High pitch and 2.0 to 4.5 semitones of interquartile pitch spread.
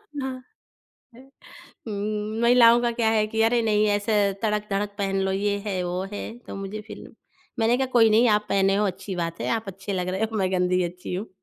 Yes: high, 210 Hz; narrow, 2.6 semitones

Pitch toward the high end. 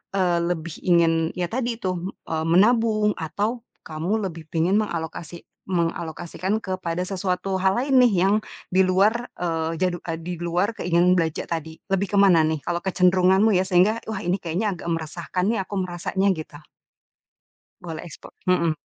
No: medium, 180 Hz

